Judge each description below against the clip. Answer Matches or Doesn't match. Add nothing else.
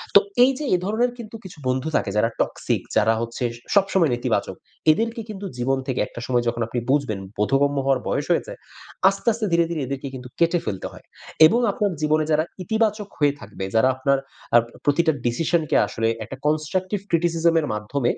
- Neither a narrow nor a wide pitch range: Doesn't match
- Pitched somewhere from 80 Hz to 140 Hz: Doesn't match